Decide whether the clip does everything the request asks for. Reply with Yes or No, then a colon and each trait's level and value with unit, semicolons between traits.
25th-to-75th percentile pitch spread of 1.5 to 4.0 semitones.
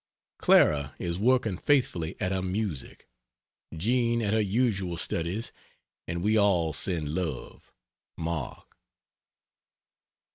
No: average, 4.7 semitones